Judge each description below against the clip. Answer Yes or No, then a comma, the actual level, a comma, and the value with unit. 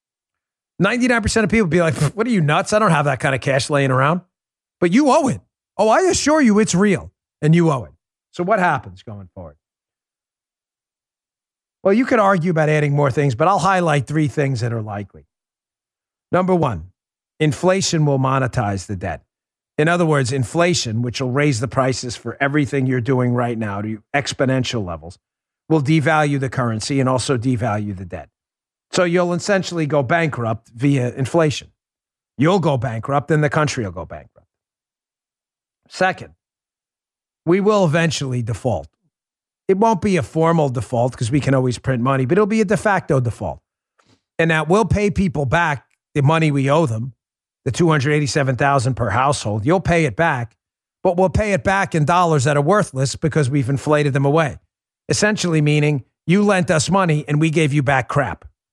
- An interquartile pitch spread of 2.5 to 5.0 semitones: No, wide, 5.4 semitones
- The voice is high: No, medium, 145 Hz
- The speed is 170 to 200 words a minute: Yes, average, 175 wpm